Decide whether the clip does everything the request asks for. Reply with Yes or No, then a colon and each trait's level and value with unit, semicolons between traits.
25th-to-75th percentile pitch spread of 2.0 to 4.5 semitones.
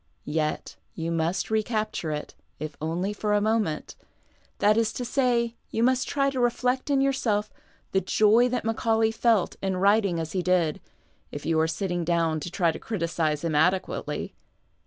No: wide, 5.4 semitones